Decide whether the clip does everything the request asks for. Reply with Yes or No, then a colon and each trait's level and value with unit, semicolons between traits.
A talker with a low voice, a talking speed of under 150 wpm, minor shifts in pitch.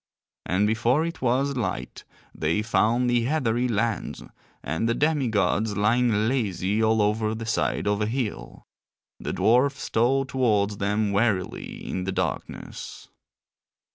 No: low, 110 Hz; average, 140 wpm; average, 3.2 semitones